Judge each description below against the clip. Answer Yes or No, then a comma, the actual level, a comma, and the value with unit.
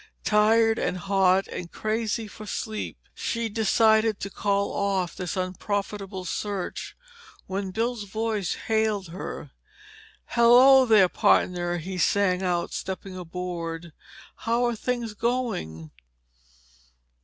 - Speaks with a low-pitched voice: No, high, 200 Hz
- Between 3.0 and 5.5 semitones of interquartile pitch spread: Yes, average, 3.4 semitones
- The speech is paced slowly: Yes, slow, 110 wpm